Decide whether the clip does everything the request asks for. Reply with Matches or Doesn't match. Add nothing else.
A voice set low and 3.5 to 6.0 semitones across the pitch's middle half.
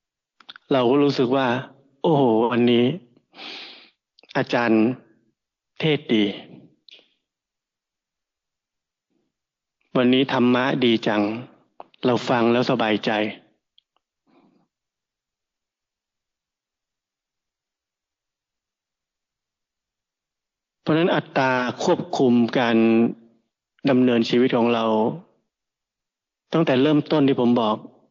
Doesn't match